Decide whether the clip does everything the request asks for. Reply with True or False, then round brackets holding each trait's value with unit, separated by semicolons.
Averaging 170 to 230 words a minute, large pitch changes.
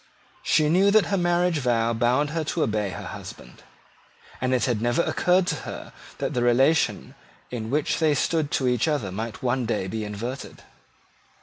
True (180 wpm; 5.8 semitones)